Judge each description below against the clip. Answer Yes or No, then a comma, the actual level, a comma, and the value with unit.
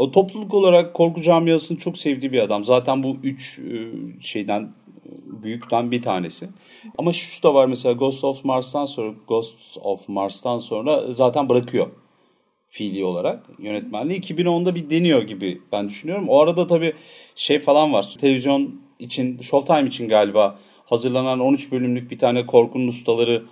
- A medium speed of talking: No, fast, 145 wpm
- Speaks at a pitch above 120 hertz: Yes, low, 135 Hz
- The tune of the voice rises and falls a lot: Yes, wide, 5.8 semitones